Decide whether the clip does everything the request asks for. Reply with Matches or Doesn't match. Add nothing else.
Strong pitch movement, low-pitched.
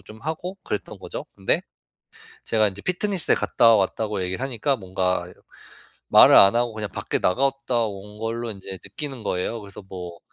Doesn't match